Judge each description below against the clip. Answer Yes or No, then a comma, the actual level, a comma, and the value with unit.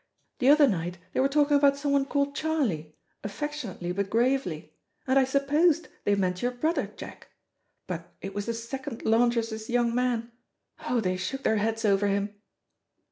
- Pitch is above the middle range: Yes, high, 235 Hz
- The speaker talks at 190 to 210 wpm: No, average, 165 wpm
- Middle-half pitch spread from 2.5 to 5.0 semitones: No, wide, 5.6 semitones